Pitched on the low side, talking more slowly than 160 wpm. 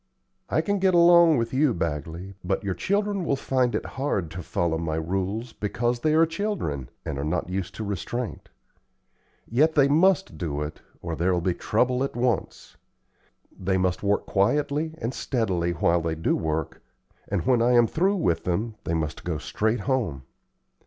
No: low, 110 Hz; average, 175 wpm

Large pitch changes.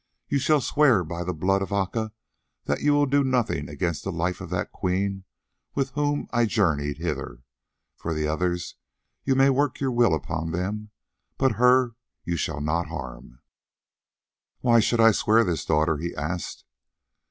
Yes: wide, 7.0 semitones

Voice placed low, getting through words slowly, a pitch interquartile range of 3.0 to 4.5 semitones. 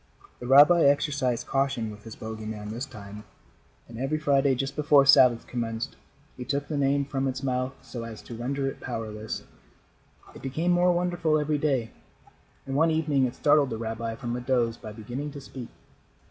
No: low, 130 Hz; average, 185 wpm; average, 3.7 semitones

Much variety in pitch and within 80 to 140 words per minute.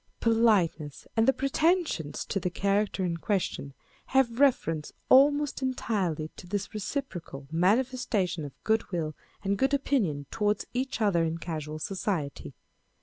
Yes: wide, 7.3 semitones; slow, 135 wpm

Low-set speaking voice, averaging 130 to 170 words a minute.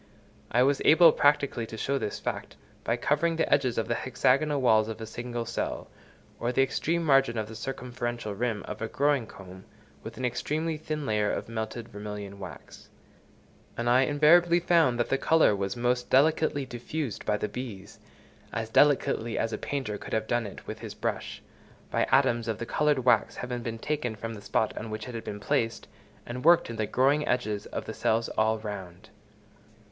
No: low, 120 Hz; average, 190 wpm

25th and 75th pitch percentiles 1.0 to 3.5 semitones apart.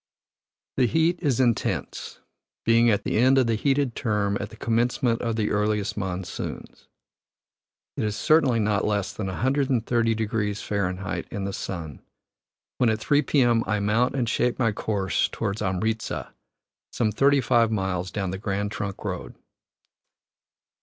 Yes: average, 3.2 semitones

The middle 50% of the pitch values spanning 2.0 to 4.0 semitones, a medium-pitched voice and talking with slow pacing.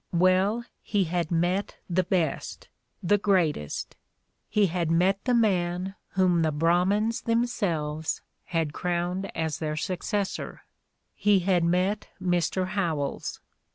Yes: average, 2.9 semitones; medium, 180 Hz; slow, 125 wpm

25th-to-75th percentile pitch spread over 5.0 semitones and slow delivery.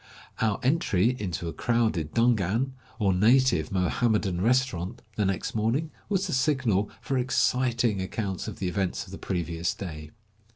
No: wide, 5.4 semitones; average, 155 wpm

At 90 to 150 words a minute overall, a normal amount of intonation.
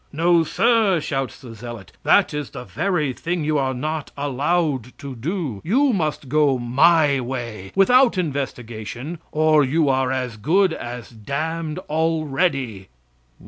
Yes: average, 140 wpm; average, 4.6 semitones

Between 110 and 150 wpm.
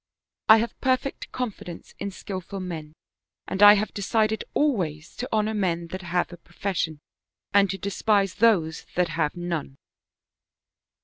Yes: average, 145 wpm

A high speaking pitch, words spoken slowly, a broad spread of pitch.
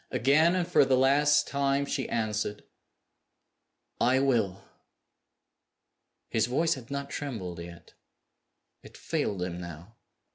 No: low, 125 Hz; slow, 115 wpm; wide, 6.0 semitones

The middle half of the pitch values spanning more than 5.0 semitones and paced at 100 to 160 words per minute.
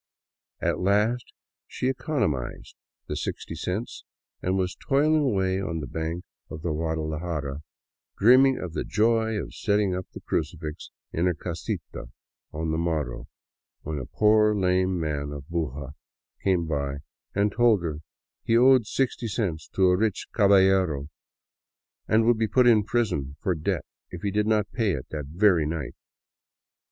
Yes: wide, 5.4 semitones; average, 155 wpm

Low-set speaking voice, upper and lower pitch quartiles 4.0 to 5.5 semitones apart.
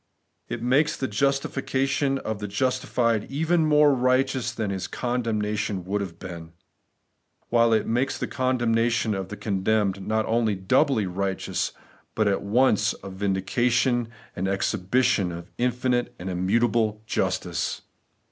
Yes: low, 115 Hz; average, 4.4 semitones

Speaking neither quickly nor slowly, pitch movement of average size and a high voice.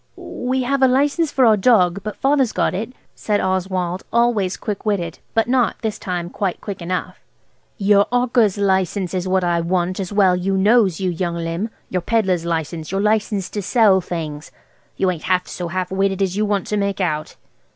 Yes: average, 190 wpm; average, 3.2 semitones; high, 195 Hz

